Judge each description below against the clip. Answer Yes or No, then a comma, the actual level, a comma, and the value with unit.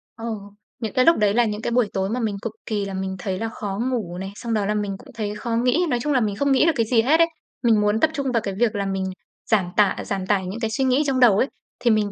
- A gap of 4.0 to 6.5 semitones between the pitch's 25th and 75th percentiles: No, average, 3.5 semitones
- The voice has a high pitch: Yes, high, 220 Hz